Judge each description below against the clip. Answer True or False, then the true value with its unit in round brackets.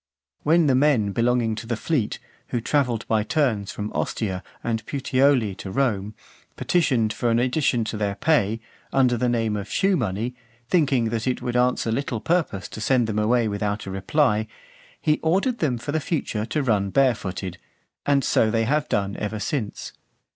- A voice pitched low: True (120 Hz)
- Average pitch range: True (4.5 semitones)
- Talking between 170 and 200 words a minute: True (175 wpm)